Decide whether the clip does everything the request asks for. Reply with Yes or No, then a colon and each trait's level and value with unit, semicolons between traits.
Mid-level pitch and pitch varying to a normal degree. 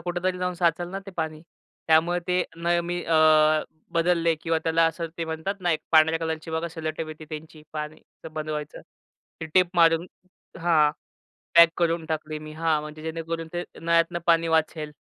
No: medium, 165 Hz; narrow, 1.4 semitones